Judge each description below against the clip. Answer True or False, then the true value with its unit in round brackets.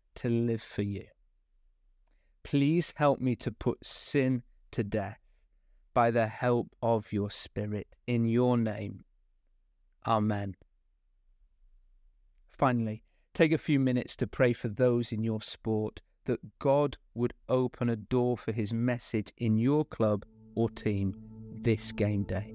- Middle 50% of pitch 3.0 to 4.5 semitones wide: True (3.6 semitones)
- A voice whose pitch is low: True (110 Hz)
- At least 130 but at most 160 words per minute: True (135 wpm)